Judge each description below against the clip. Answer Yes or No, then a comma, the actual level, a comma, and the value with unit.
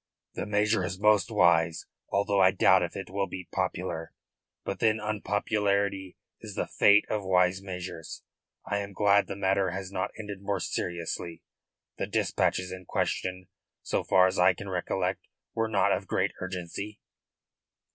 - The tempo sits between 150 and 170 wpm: Yes, average, 155 wpm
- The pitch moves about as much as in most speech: No, narrow, 1.9 semitones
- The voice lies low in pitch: Yes, very low, 95 Hz